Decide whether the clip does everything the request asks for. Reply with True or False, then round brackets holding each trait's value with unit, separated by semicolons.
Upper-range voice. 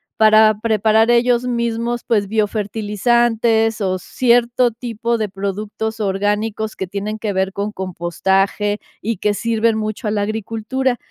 True (215 Hz)